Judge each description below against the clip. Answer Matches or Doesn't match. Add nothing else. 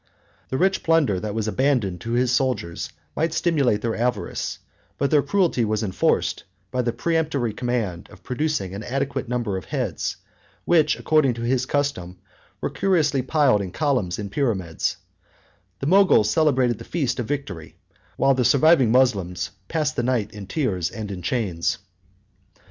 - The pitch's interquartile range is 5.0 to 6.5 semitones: Matches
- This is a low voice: Matches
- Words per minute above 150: Matches